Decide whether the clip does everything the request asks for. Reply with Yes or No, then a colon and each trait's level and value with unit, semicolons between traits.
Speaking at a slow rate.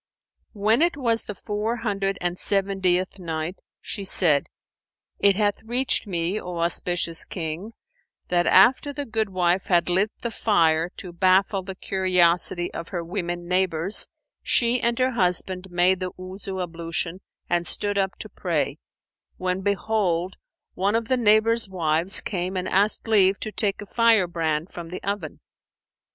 No: average, 150 wpm